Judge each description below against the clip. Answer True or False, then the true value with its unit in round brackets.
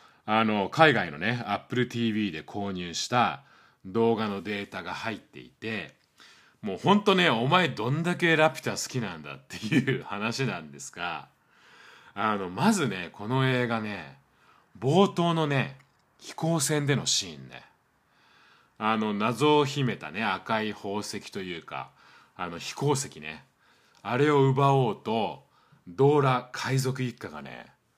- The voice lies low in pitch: True (120 Hz)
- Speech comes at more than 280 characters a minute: False (260 characters per minute)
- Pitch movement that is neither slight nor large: False (5.7 semitones)